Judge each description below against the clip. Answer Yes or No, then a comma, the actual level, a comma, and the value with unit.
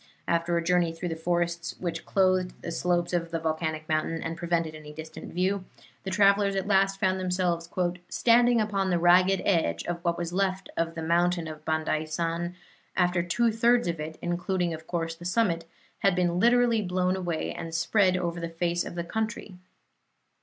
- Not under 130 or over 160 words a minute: No, average, 180 wpm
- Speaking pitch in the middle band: Yes, medium, 175 Hz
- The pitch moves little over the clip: Yes, narrow, 2.2 semitones